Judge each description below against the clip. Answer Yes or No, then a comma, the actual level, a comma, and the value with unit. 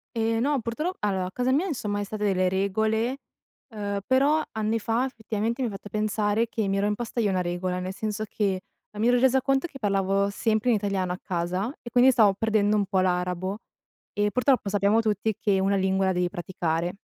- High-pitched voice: Yes, high, 210 Hz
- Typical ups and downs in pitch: Yes, average, 3.2 semitones